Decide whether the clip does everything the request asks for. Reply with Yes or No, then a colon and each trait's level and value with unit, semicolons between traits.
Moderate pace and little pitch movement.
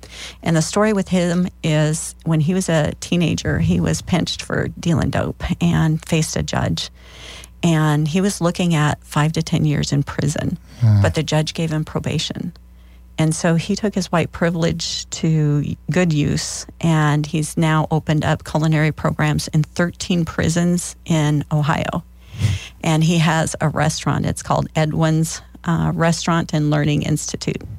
Yes: average, 160 wpm; narrow, 2.0 semitones